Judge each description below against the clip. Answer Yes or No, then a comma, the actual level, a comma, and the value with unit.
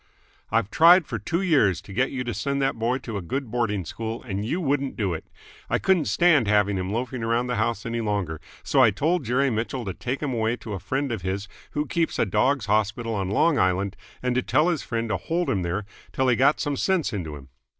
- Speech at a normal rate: No, fast, 240 wpm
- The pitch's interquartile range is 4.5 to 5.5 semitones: Yes, average, 5.1 semitones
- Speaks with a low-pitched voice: Yes, low, 115 Hz